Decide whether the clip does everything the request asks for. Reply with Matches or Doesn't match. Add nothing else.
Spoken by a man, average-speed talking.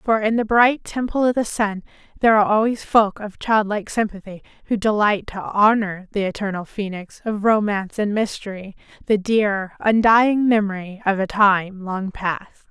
Doesn't match